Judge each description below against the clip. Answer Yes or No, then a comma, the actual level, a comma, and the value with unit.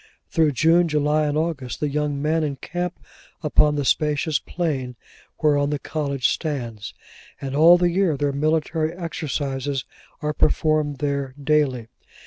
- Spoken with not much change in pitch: Yes, narrow, 2.2 semitones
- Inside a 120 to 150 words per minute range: Yes, slow, 135 wpm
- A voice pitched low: No, medium, 150 Hz